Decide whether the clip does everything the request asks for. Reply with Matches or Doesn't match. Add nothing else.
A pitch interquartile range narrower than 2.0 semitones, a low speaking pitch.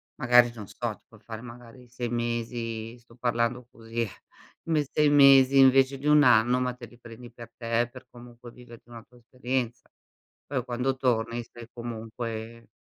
Matches